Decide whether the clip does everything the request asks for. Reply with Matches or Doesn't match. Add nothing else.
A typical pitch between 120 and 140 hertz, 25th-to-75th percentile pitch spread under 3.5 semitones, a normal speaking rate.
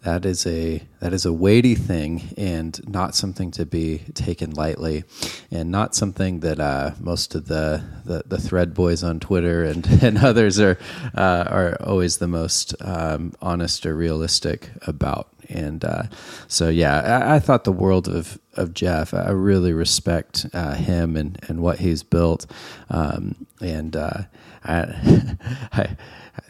Doesn't match